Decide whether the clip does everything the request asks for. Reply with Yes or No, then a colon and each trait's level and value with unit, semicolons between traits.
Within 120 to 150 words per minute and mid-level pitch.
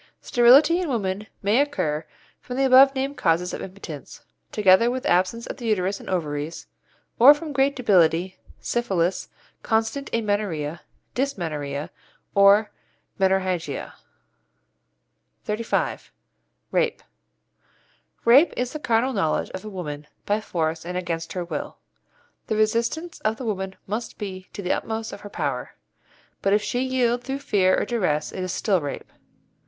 No: average, 145 wpm; high, 205 Hz